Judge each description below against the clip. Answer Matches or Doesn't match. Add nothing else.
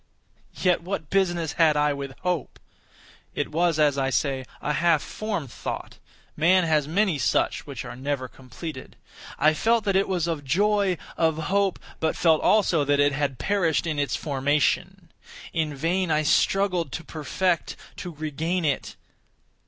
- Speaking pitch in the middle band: Matches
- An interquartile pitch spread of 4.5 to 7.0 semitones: Doesn't match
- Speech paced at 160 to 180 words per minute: Doesn't match